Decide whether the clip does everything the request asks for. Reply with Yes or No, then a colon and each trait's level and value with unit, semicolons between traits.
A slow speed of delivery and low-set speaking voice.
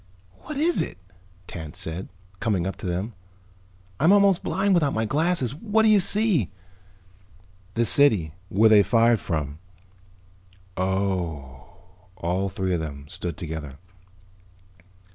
Yes: slow, 125 wpm; low, 100 Hz